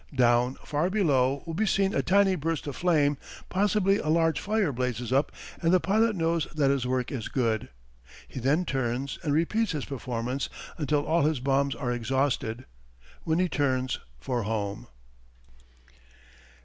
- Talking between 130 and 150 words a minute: No, average, 160 wpm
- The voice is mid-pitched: Yes, medium, 145 Hz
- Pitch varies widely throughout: No, average, 4.9 semitones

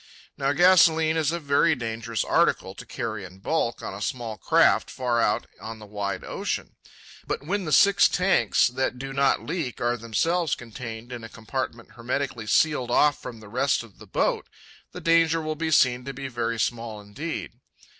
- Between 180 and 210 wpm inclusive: Yes, average, 185 wpm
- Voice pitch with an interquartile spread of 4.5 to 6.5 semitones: Yes, wide, 5.4 semitones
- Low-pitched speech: Yes, low, 125 Hz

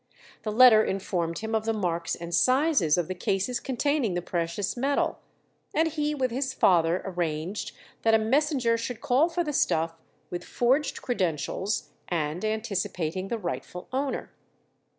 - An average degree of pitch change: No, wide, 6.6 semitones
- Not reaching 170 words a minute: Yes, average, 150 wpm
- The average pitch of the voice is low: No, high, 215 Hz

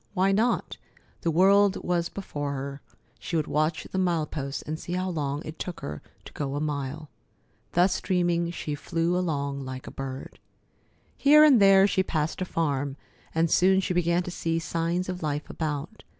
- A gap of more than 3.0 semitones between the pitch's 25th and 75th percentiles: Yes, average, 3.9 semitones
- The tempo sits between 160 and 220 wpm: Yes, average, 180 wpm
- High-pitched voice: No, medium, 165 Hz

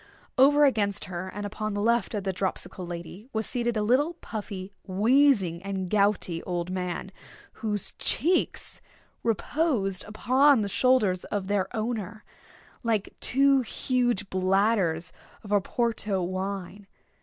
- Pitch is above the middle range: Yes, high, 205 Hz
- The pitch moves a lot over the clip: No, average, 4.0 semitones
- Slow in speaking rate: Yes, slow, 130 wpm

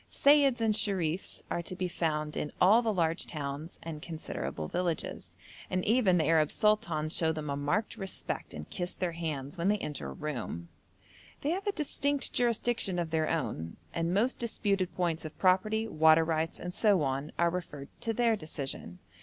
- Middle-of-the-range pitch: Yes, medium, 170 Hz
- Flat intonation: No, average, 5.3 semitones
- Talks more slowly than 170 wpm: No, average, 180 wpm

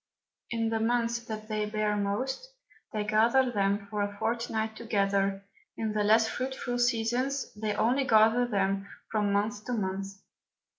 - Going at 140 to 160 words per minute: Yes, average, 150 wpm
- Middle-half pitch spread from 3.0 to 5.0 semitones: No, narrow, 2.5 semitones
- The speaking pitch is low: No, high, 220 Hz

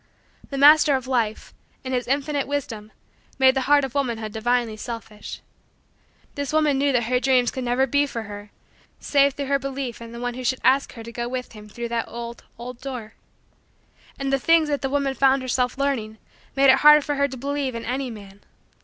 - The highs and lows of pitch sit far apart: No, average, 2.8 semitones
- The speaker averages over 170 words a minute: Yes, fast, 205 wpm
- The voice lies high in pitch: Yes, very high, 260 Hz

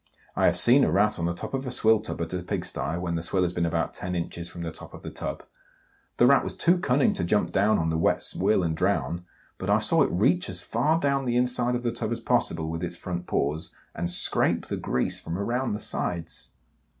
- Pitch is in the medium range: No, very low, 90 Hz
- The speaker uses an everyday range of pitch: No, wide, 5.8 semitones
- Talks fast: Yes, fast, 245 wpm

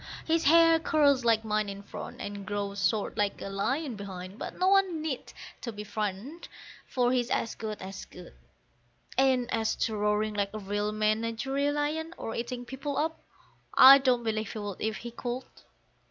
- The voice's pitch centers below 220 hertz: No, high, 230 Hz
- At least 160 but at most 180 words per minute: Yes, average, 175 wpm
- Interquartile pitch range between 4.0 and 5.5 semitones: Yes, average, 5.0 semitones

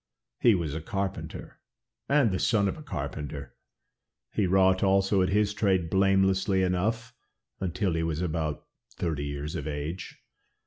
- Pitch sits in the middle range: No, very low, 95 Hz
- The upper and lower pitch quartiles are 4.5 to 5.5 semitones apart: No, average, 3.4 semitones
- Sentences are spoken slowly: No, average, 145 wpm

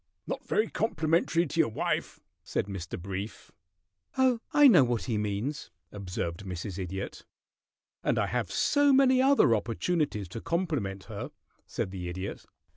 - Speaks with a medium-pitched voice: No, low, 115 Hz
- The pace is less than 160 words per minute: Yes, average, 145 wpm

